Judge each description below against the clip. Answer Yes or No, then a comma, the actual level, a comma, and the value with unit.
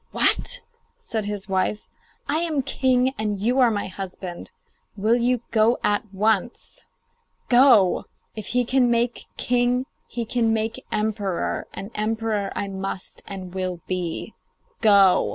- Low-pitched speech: No, high, 220 Hz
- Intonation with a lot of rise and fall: No, average, 3.8 semitones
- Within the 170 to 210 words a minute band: No, slow, 135 wpm